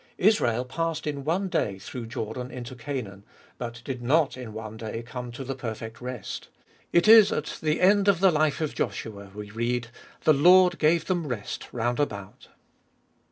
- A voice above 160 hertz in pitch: No, low, 125 Hz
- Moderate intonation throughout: No, wide, 6.0 semitones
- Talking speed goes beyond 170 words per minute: Yes, average, 180 wpm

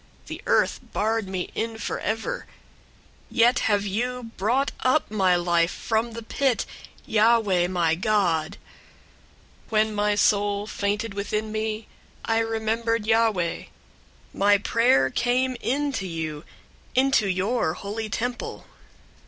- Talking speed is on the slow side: Yes, slow, 120 wpm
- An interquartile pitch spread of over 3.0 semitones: No, average, 2.7 semitones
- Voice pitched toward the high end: Yes, high, 215 Hz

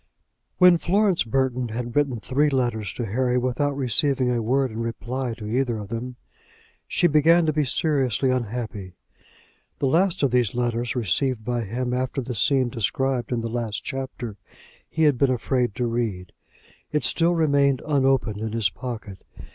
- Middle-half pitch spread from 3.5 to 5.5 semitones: No, average, 3.0 semitones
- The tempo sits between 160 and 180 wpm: Yes, average, 165 wpm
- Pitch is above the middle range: No, low, 125 Hz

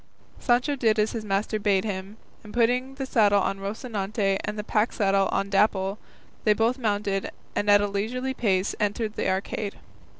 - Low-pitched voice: No, high, 210 Hz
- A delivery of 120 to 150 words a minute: No, average, 175 wpm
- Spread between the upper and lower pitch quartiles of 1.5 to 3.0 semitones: Yes, narrow, 2.4 semitones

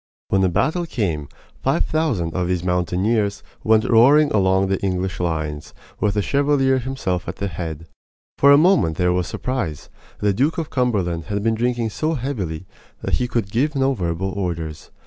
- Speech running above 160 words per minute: Yes, average, 175 wpm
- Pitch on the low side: Yes, low, 100 Hz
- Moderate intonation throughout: No, wide, 6.6 semitones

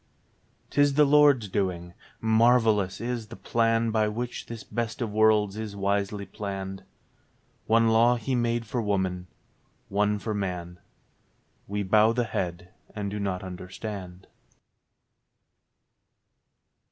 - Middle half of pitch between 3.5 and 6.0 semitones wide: No, average, 3.0 semitones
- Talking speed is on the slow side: Yes, slow, 120 wpm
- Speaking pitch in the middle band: No, low, 105 Hz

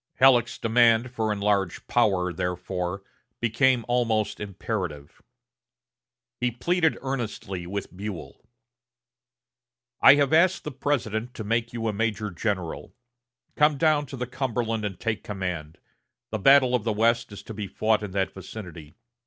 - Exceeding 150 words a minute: No, average, 140 wpm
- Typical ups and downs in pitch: Yes, average, 4.0 semitones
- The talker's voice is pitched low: Yes, low, 110 Hz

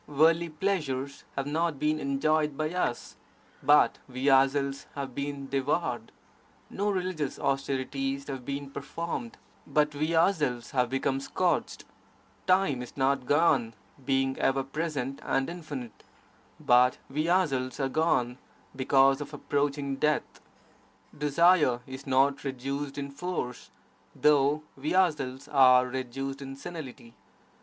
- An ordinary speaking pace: No, slow, 125 wpm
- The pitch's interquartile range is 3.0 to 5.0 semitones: No, narrow, 2.4 semitones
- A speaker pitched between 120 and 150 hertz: Yes, medium, 140 Hz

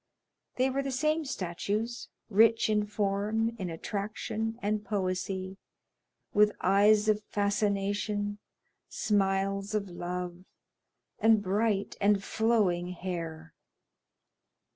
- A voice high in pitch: Yes, high, 205 Hz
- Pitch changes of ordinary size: No, narrow, 2.1 semitones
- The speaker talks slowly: Yes, slow, 100 wpm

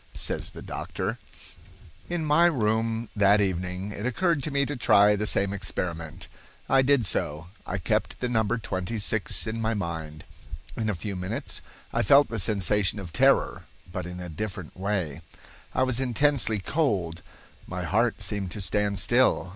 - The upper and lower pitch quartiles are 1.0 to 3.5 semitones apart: No, average, 4.4 semitones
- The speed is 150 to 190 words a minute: Yes, average, 165 wpm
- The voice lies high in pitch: No, low, 105 Hz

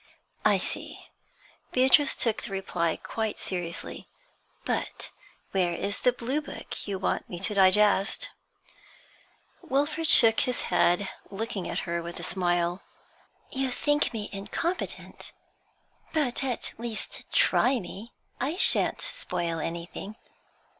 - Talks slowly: Yes, slow, 120 wpm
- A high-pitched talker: Yes, high, 210 Hz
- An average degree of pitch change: No, wide, 6.2 semitones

